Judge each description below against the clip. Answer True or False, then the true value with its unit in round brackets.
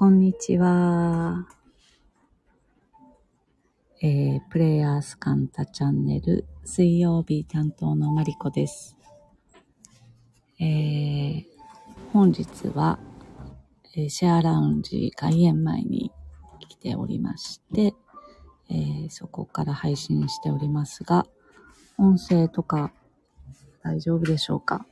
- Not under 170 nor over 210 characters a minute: True (185 characters per minute)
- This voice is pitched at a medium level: True (150 Hz)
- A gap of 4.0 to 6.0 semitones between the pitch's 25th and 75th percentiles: True (5.6 semitones)